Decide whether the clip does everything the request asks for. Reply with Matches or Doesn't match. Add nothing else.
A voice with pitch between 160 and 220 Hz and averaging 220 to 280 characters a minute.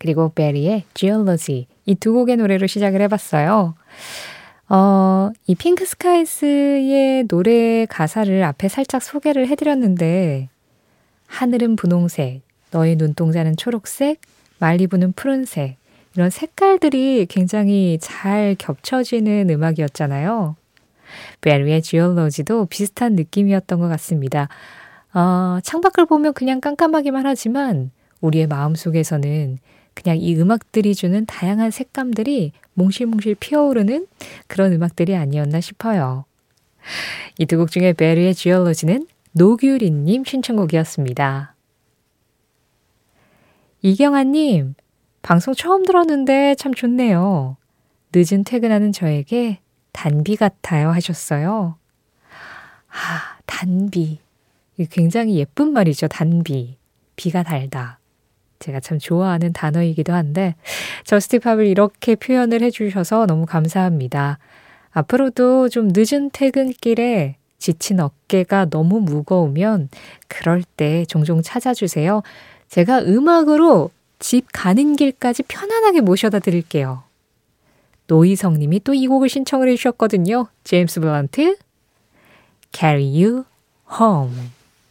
Matches